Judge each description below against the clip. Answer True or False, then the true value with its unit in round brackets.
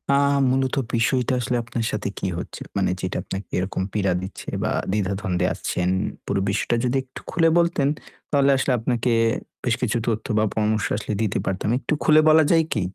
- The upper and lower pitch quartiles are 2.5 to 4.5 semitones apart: False (4.9 semitones)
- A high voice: False (115 Hz)